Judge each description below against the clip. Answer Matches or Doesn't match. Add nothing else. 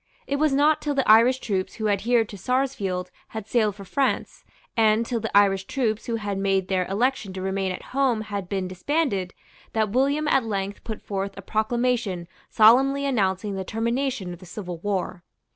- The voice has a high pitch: Matches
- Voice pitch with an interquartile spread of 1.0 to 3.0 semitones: Doesn't match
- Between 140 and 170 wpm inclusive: Doesn't match